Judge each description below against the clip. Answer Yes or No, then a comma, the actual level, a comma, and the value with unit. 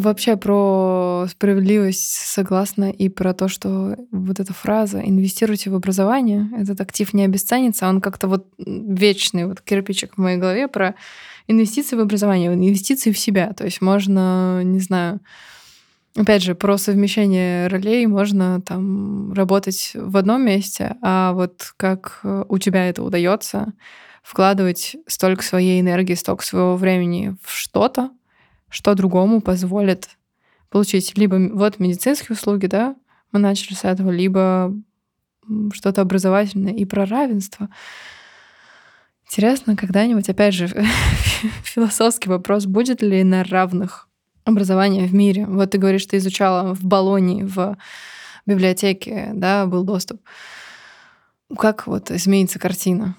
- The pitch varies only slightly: Yes, narrow, 1.9 semitones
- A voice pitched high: Yes, high, 195 Hz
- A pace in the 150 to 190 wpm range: No, average, 130 wpm